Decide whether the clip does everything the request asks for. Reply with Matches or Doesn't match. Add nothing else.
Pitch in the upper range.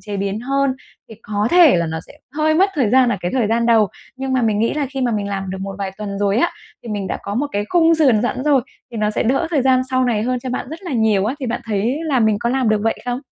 Matches